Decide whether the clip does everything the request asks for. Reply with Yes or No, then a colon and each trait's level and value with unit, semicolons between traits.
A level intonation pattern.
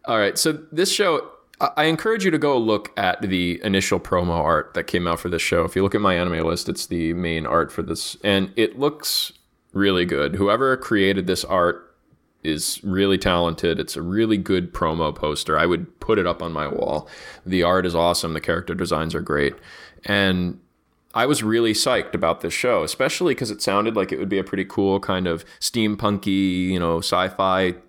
No: average, 3.5 semitones